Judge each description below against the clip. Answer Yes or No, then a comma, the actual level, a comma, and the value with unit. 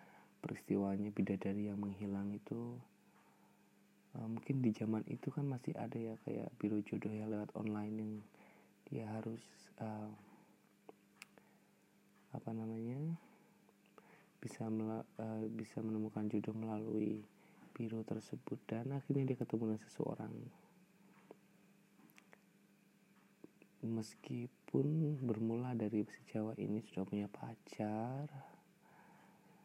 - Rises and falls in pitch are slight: Yes, narrow, 1.8 semitones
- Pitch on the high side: No, low, 110 Hz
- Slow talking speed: No, average, 100 wpm